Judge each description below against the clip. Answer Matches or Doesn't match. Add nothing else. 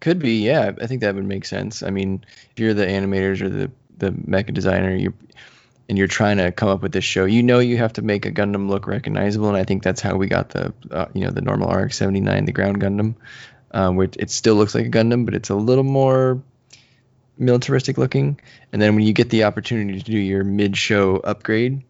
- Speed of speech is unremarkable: Doesn't match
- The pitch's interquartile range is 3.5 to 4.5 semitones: Matches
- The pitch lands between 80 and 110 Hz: Matches